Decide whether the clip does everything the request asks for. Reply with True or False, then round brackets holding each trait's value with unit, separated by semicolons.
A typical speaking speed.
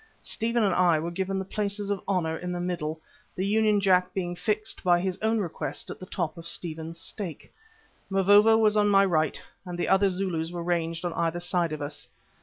False (210 wpm)